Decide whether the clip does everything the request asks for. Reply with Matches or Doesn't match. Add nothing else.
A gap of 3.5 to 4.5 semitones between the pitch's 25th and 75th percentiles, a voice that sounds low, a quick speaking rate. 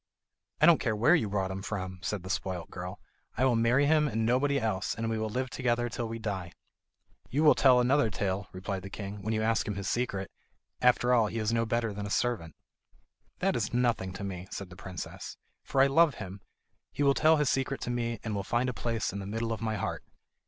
Matches